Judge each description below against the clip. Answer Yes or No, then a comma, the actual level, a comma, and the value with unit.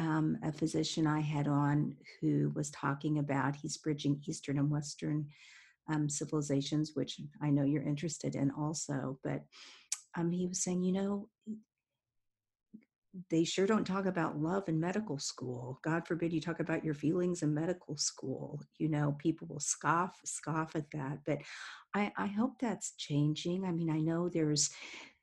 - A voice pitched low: No, medium, 155 Hz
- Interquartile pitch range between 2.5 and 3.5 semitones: Yes, average, 2.9 semitones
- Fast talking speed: No, average, 165 wpm